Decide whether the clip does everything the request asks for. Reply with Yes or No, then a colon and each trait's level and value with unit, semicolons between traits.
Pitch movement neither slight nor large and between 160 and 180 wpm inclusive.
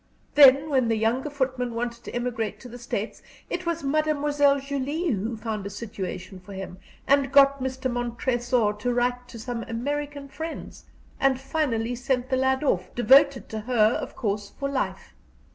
Yes: average, 3.4 semitones; average, 170 wpm